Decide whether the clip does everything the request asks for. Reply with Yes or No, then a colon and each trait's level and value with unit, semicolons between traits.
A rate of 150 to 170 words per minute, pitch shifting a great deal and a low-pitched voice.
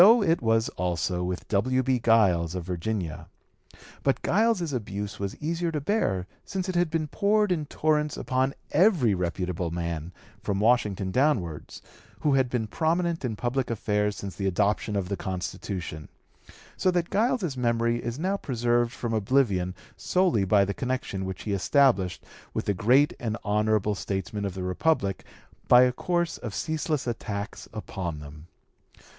Yes: average, 160 wpm; wide, 7.6 semitones; low, 115 Hz